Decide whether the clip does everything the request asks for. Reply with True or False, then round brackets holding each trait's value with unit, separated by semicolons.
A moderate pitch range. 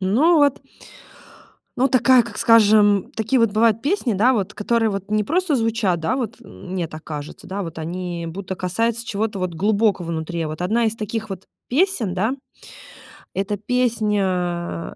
True (4.1 semitones)